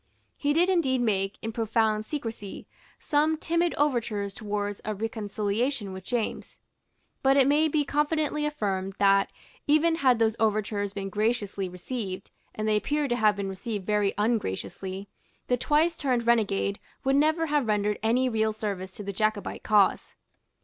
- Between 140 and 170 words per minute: Yes, average, 155 wpm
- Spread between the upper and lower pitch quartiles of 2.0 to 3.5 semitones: No, wide, 5.5 semitones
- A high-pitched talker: Yes, high, 220 Hz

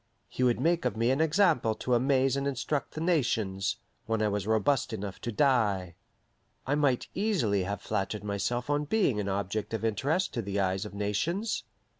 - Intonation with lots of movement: Yes, wide, 6.0 semitones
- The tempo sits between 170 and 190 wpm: Yes, average, 185 wpm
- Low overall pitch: Yes, low, 120 Hz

